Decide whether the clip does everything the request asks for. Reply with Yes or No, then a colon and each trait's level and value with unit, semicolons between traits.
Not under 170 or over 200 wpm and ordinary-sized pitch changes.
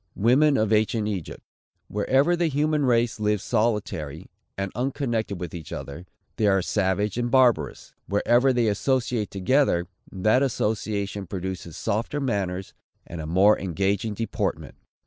No: slow, 135 wpm; average, 4.3 semitones